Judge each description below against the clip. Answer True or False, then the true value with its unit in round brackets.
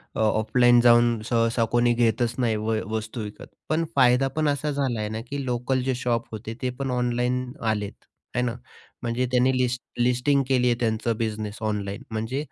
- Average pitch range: False (2.3 semitones)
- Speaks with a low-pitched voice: True (120 Hz)